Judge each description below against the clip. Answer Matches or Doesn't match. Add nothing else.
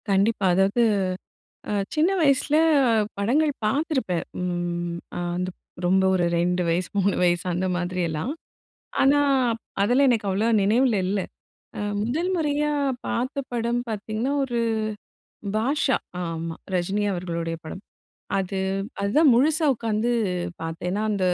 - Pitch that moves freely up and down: Matches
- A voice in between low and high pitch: Doesn't match